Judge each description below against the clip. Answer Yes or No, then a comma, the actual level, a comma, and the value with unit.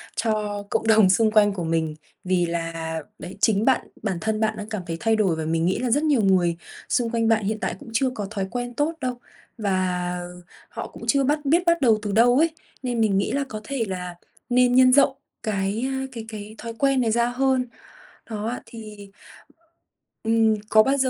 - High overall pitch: Yes, high, 220 Hz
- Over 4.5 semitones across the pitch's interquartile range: No, average, 4.2 semitones